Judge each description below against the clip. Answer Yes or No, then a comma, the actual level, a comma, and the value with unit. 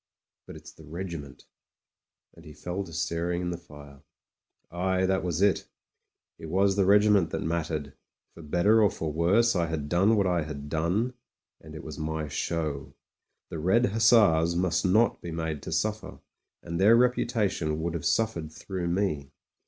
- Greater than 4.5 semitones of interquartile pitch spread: No, average, 3.7 semitones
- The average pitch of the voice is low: Yes, very low, 85 Hz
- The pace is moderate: Yes, average, 175 wpm